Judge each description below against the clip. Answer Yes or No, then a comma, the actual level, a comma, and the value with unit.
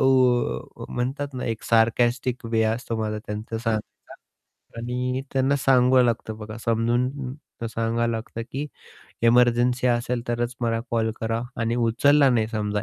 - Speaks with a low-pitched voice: Yes, low, 120 Hz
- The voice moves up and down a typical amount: No, narrow, 1.8 semitones